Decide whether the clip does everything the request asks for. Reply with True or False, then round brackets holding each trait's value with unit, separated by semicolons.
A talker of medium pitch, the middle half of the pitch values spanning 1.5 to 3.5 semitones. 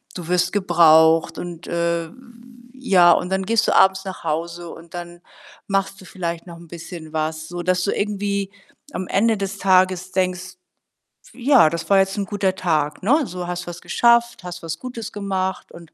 True (180 Hz; 2.5 semitones)